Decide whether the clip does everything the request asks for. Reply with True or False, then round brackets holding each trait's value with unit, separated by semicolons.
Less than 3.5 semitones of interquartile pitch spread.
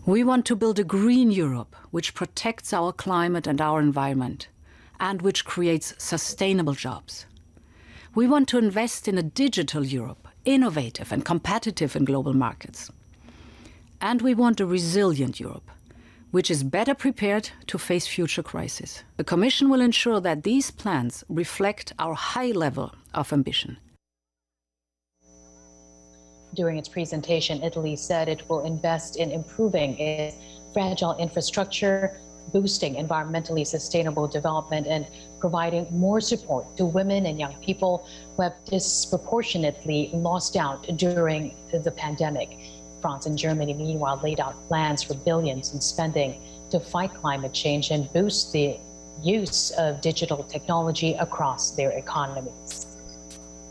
False (5.5 semitones)